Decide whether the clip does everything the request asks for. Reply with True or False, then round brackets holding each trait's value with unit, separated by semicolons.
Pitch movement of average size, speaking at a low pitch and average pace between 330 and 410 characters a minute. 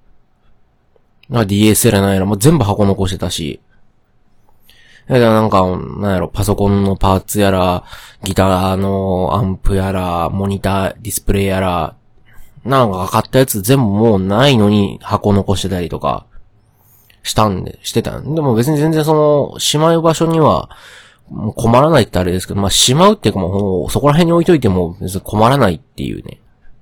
True (4.2 semitones; 105 Hz; 335 characters per minute)